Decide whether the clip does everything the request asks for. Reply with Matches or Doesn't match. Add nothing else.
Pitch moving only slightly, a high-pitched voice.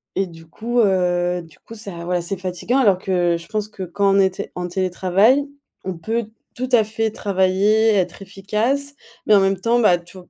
Doesn't match